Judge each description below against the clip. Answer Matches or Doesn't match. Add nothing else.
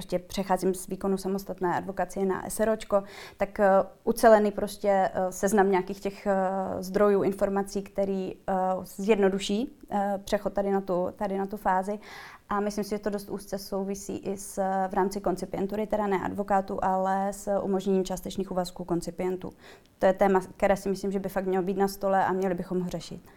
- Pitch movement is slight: Matches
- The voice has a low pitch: Doesn't match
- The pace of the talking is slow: Doesn't match